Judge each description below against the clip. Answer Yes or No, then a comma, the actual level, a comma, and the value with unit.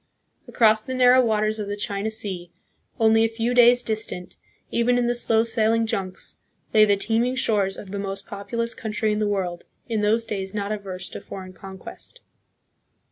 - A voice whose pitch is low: No, high, 215 Hz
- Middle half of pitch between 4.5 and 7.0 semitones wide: No, narrow, 2.5 semitones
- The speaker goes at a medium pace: Yes, average, 180 wpm